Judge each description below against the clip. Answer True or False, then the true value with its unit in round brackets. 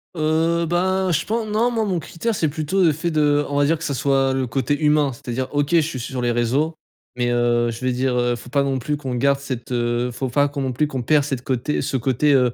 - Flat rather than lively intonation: False (3.9 semitones)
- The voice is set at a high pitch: False (140 Hz)